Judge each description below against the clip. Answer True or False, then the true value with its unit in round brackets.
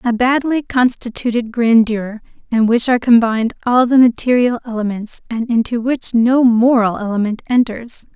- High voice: True (235 Hz)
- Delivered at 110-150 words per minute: True (140 wpm)